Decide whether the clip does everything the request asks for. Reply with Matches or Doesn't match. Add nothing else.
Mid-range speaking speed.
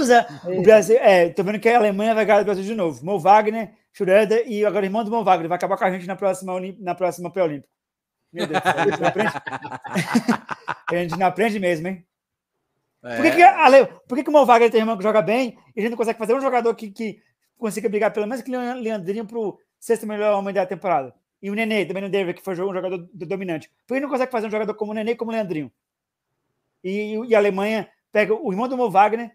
Doesn't match